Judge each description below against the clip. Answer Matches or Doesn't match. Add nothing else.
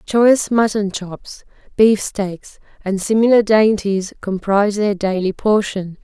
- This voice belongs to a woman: Matches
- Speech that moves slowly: Matches